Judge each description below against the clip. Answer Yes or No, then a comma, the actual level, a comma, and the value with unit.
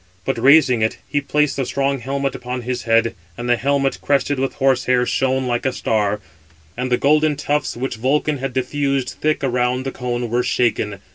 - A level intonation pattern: Yes, narrow, 2.3 semitones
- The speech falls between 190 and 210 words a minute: Yes, average, 195 wpm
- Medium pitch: No, low, 130 Hz